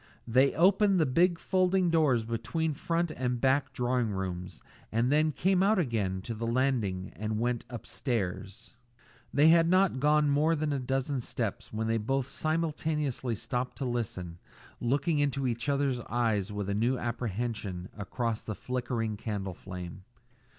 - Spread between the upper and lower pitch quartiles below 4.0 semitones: No, average, 5.2 semitones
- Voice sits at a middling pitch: No, low, 125 Hz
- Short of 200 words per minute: Yes, average, 160 wpm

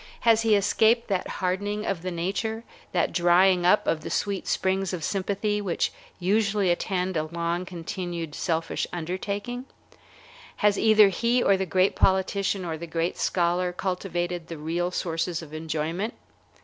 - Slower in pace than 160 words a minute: Yes, average, 150 wpm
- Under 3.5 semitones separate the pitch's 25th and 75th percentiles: Yes, average, 2.8 semitones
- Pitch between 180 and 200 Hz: Yes, medium, 185 Hz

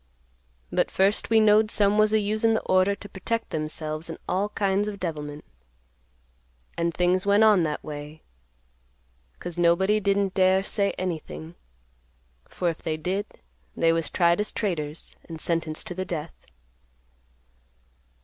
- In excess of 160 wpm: No, average, 145 wpm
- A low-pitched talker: No, medium, 185 Hz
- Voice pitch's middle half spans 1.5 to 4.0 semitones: Yes, average, 3.7 semitones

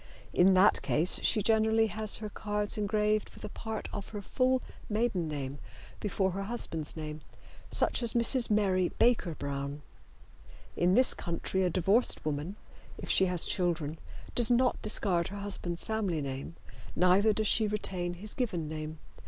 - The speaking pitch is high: Yes, high, 195 Hz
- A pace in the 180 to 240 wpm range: No, average, 160 wpm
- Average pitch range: Yes, average, 4.3 semitones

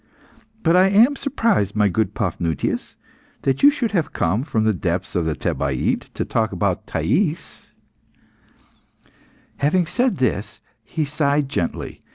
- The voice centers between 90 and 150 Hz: Yes, low, 135 Hz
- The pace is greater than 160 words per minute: No, average, 140 wpm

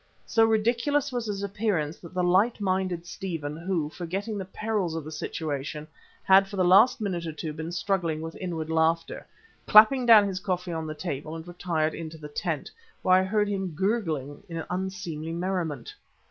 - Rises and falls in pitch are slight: No, average, 3.8 semitones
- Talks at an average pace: Yes, average, 180 wpm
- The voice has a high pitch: No, medium, 180 Hz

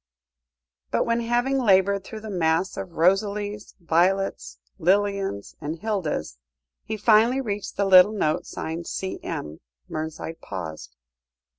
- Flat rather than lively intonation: No, average, 4.6 semitones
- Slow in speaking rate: Yes, slow, 120 wpm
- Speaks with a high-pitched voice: Yes, high, 195 Hz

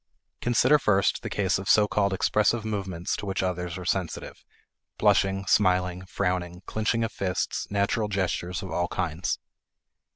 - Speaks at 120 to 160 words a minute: Yes, average, 150 wpm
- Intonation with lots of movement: No, narrow, 2.4 semitones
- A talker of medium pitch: No, very low, 95 Hz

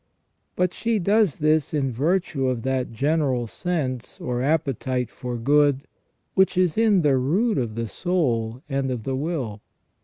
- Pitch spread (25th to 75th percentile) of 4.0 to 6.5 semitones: Yes, wide, 5.5 semitones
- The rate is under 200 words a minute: Yes, average, 155 wpm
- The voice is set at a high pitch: No, medium, 140 Hz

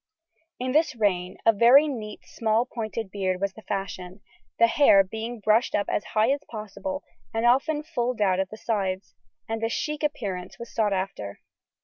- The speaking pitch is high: Yes, high, 220 Hz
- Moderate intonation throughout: Yes, average, 3.7 semitones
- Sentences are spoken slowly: No, average, 175 wpm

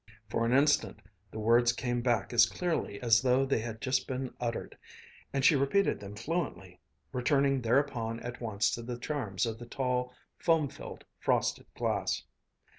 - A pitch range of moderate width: Yes, average, 3.0 semitones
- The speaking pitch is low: Yes, low, 120 Hz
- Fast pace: No, average, 165 wpm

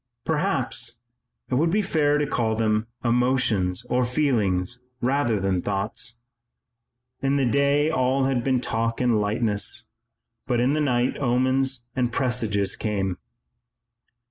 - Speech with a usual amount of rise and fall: Yes, average, 3.7 semitones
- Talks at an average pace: No, slow, 130 wpm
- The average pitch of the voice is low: Yes, low, 120 Hz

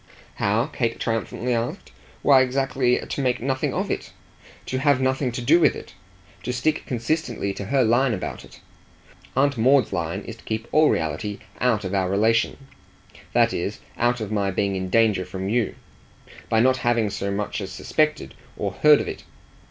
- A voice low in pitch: Yes, low, 120 Hz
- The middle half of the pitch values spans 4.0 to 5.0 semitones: Yes, average, 4.3 semitones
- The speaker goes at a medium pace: Yes, average, 180 wpm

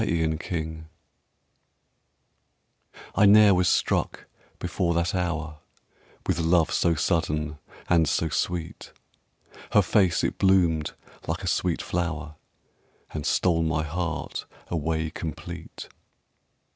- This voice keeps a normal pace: No, slow, 105 wpm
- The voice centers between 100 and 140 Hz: No, very low, 80 Hz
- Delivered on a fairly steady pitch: Yes, narrow, 1.9 semitones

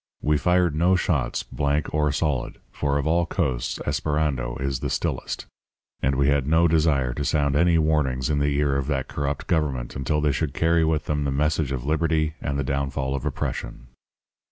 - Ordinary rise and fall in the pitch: No, narrow, 2.3 semitones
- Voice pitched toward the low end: Yes, very low, 75 Hz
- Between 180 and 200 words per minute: Yes, average, 190 wpm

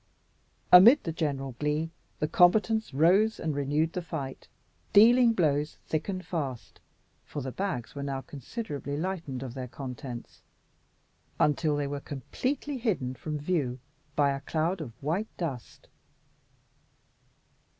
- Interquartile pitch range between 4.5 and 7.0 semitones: Yes, average, 5.0 semitones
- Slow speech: Yes, slow, 130 wpm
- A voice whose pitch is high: No, medium, 150 Hz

